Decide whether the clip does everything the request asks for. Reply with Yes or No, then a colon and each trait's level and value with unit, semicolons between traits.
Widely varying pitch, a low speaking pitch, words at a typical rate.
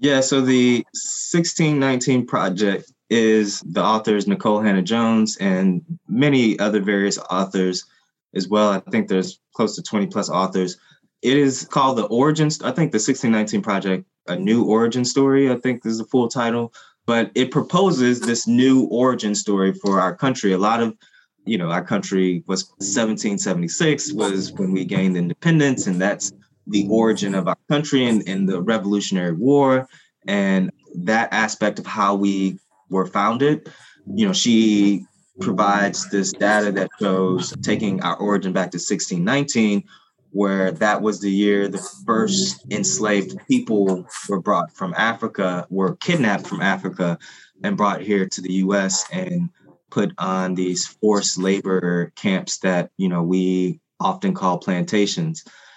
Yes: wide, 6.0 semitones; low, 105 Hz; average, 150 wpm